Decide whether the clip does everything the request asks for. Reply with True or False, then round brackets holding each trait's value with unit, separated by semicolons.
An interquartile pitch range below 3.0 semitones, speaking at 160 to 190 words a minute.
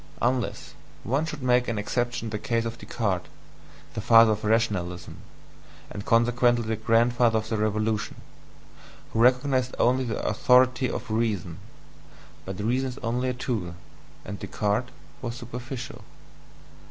False (2.4 semitones; 140 wpm)